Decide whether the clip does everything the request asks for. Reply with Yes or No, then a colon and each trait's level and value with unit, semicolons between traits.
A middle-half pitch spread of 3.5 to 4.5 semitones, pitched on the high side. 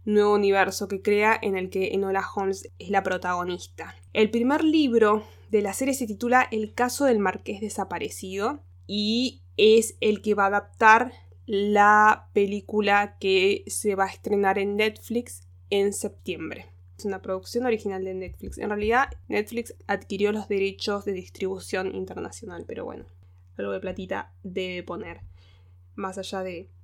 No: average, 2.8 semitones; high, 200 Hz